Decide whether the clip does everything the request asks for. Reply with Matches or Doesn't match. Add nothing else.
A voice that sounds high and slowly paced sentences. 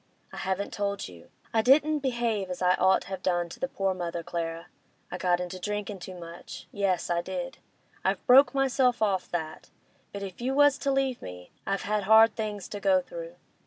Doesn't match